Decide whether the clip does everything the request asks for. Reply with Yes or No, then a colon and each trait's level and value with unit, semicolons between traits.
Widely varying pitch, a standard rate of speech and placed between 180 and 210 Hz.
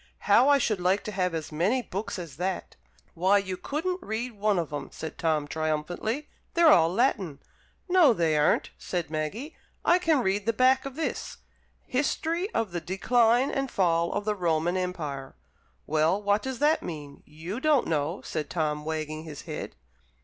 Yes: wide, 7.7 semitones; average, 175 wpm; high, 190 Hz